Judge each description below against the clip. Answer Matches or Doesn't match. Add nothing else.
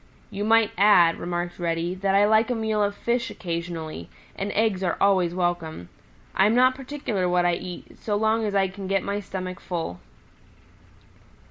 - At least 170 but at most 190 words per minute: Matches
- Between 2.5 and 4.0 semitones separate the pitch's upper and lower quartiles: Matches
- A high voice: Matches